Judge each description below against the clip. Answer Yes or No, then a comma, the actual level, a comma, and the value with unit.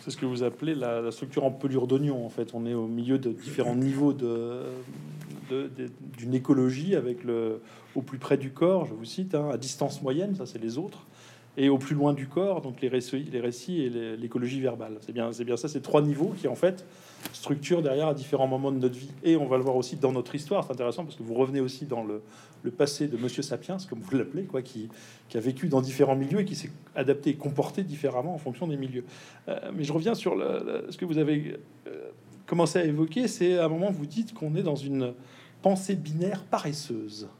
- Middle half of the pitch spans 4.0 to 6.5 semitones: Yes, average, 4.4 semitones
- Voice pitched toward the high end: No, low, 135 Hz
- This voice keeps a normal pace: No, fast, 240 wpm